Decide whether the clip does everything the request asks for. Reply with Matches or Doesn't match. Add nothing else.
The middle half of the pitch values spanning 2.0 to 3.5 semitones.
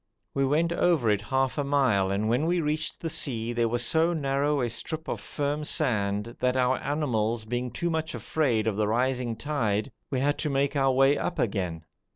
Doesn't match